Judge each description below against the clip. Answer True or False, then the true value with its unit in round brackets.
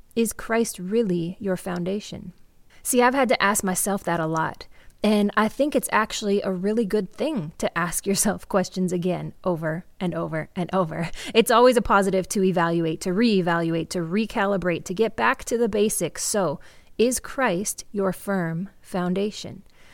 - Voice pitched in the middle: False (195 Hz)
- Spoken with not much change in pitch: False (3.3 semitones)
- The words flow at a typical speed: True (165 wpm)